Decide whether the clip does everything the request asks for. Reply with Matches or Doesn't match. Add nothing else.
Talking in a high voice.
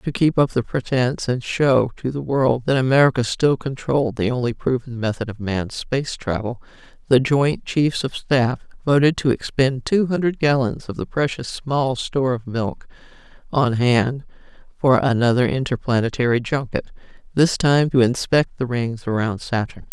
Doesn't match